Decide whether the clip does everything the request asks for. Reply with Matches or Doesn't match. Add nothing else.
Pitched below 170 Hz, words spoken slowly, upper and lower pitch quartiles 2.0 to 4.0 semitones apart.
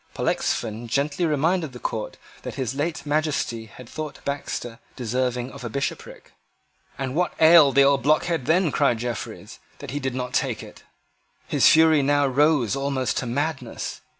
Doesn't match